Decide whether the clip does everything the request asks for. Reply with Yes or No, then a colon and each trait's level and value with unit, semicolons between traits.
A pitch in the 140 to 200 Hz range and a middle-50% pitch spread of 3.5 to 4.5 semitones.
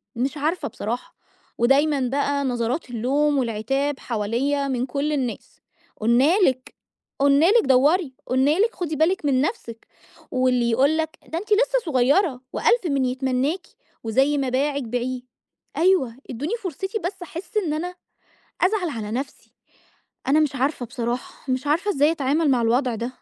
No: very high, 275 Hz; average, 4.0 semitones